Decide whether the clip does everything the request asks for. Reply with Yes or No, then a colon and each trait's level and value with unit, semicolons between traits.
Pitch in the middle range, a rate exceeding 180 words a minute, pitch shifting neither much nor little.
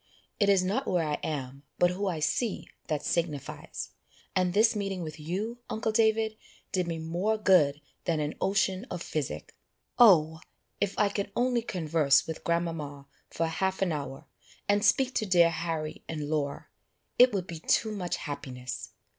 No: medium, 175 Hz; average, 165 wpm; average, 4.7 semitones